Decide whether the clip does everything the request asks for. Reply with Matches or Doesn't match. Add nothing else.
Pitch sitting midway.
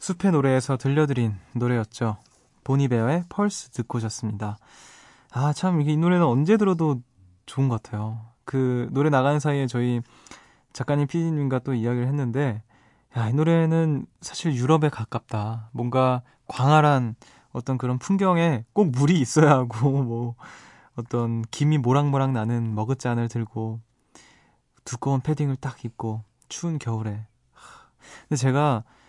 Doesn't match